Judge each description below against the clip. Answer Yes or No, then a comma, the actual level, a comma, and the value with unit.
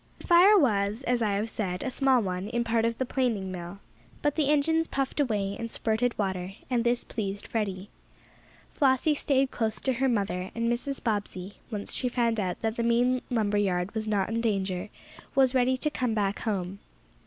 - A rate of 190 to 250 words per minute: Yes, average, 195 wpm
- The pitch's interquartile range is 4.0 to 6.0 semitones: Yes, average, 4.3 semitones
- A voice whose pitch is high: Yes, high, 225 Hz